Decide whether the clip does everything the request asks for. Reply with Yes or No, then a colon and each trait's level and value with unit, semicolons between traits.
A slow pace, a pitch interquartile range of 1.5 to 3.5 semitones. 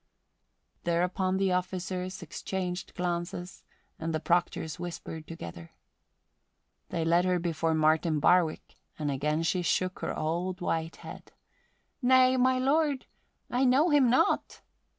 Yes: slow, 125 wpm; average, 2.8 semitones